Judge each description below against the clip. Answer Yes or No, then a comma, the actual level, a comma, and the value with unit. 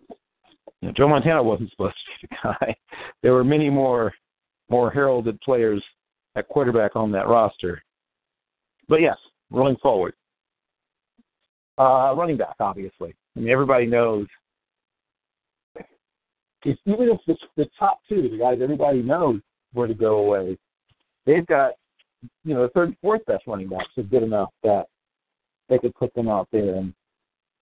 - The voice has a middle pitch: No, low, 120 Hz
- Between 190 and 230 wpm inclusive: No, average, 150 wpm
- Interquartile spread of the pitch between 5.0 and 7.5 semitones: Yes, wide, 5.5 semitones